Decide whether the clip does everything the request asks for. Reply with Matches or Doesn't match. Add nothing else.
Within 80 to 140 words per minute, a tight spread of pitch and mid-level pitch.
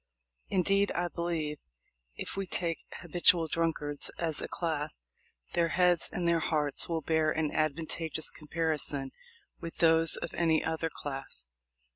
Matches